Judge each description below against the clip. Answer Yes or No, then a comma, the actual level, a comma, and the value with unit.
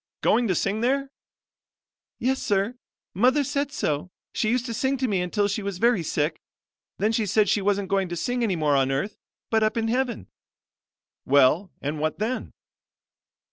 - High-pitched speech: Yes, high, 210 Hz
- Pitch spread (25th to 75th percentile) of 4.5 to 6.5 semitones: Yes, average, 5.3 semitones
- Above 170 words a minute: Yes, average, 180 wpm